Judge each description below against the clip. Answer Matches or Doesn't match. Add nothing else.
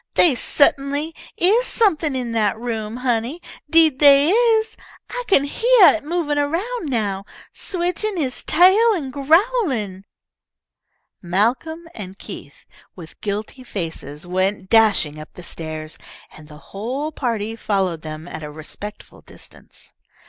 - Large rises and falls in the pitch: Matches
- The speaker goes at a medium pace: Doesn't match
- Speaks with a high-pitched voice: Matches